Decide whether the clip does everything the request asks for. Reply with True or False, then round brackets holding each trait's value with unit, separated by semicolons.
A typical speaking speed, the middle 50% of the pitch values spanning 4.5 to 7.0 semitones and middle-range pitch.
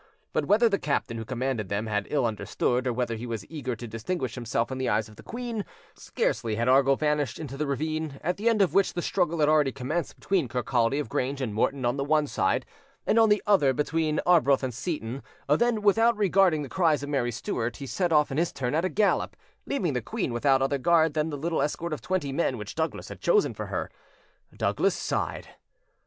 False (225 wpm; 5.5 semitones; 145 Hz)